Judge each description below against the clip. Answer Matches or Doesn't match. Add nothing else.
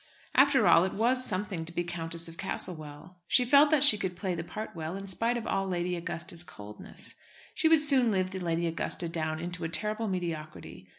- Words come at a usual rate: Doesn't match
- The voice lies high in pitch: Doesn't match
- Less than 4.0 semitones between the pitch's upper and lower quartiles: Doesn't match